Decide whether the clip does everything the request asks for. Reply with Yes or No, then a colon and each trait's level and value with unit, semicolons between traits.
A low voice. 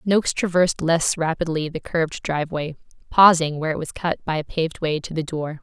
No: medium, 160 Hz